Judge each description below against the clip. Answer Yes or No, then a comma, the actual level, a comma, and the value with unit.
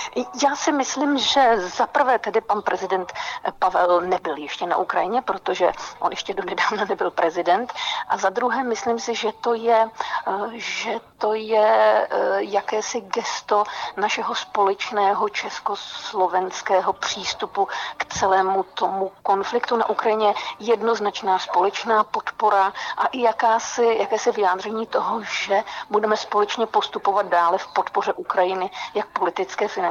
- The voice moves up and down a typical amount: Yes, average, 3.3 semitones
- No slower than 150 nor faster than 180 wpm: No, average, 130 wpm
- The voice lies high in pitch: Yes, high, 215 Hz